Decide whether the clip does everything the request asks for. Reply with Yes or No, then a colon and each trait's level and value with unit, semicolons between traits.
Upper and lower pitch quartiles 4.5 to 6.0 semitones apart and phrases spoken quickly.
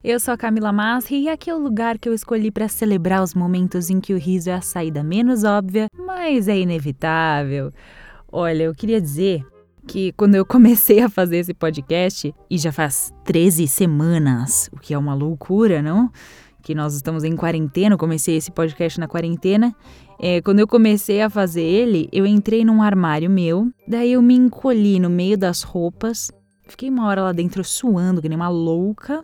Yes: average, 4.9 semitones; fast, 190 wpm